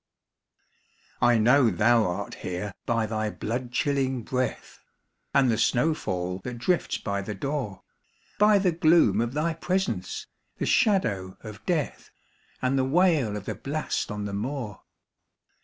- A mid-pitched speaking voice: No, low, 120 Hz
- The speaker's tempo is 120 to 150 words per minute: Yes, average, 145 wpm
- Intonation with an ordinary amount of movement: No, wide, 6.1 semitones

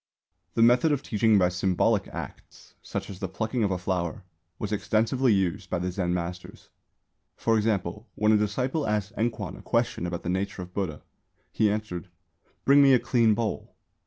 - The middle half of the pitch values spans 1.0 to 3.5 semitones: No, average, 3.9 semitones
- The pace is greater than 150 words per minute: Yes, average, 185 wpm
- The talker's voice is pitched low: Yes, low, 105 Hz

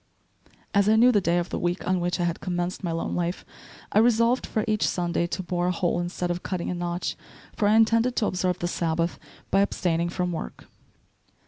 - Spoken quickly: Yes, fast, 215 wpm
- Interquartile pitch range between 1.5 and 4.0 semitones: Yes, average, 2.8 semitones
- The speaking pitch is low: No, medium, 180 Hz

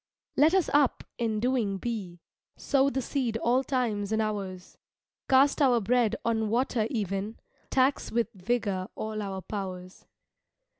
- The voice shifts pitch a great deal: No, average, 4.1 semitones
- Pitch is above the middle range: Yes, high, 225 Hz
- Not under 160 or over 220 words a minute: No, average, 140 wpm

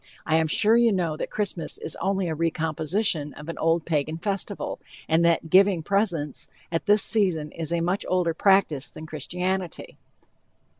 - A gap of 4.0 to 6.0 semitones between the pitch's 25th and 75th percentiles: No, average, 3.5 semitones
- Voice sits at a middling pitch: Yes, medium, 170 Hz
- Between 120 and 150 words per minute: No, average, 165 wpm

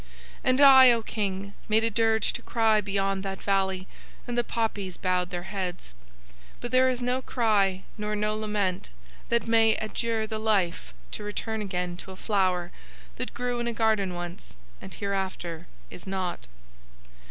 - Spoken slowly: No, average, 165 wpm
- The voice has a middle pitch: No, high, 205 Hz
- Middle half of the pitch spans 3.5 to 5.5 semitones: No, average, 3.1 semitones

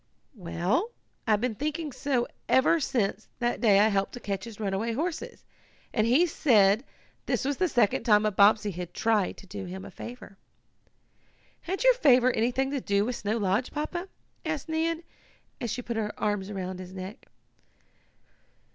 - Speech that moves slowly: No, average, 170 wpm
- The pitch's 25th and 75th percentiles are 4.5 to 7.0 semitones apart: Yes, average, 5.3 semitones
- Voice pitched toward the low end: No, high, 225 Hz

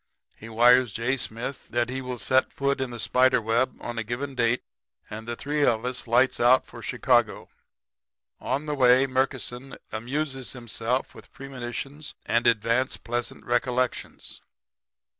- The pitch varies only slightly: Yes, narrow, 2.0 semitones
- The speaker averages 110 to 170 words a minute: Yes, average, 150 wpm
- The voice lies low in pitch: Yes, low, 125 Hz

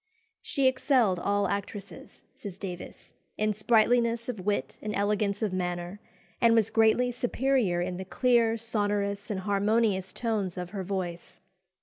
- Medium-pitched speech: No, high, 205 Hz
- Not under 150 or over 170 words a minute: No, average, 140 wpm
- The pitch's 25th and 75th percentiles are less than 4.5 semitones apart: Yes, average, 3.3 semitones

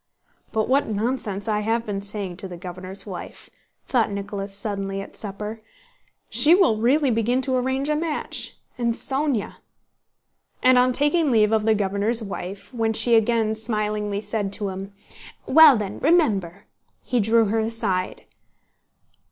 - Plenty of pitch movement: No, average, 3.7 semitones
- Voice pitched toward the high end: Yes, high, 220 Hz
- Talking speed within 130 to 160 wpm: Yes, average, 150 wpm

